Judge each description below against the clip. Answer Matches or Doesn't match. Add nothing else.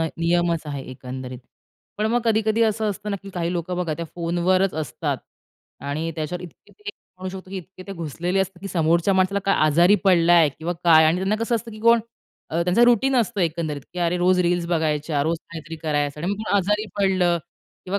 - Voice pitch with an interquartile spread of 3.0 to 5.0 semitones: Matches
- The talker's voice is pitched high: Doesn't match